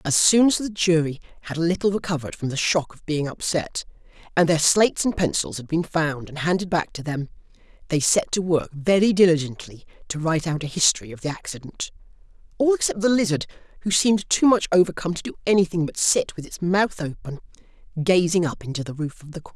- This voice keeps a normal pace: No, fast, 210 wpm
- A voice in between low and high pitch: Yes, medium, 170 Hz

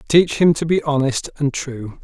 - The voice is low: No, medium, 145 Hz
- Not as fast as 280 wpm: Yes, fast, 205 wpm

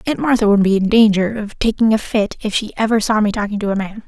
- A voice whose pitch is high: Yes, high, 215 Hz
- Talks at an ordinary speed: No, fast, 280 wpm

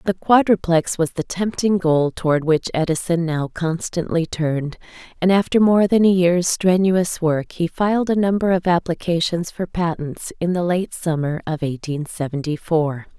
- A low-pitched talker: No, medium, 170 Hz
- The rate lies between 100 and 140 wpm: No, average, 165 wpm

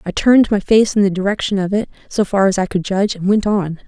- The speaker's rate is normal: No, fast, 280 wpm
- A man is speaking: No, female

